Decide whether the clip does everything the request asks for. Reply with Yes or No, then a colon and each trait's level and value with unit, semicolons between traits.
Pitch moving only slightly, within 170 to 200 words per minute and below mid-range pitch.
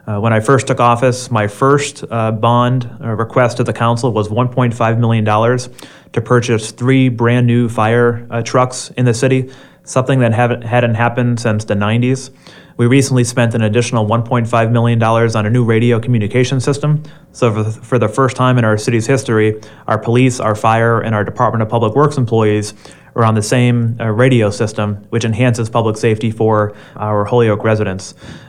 Yes: narrow, 2.3 semitones; average, 180 wpm; low, 120 Hz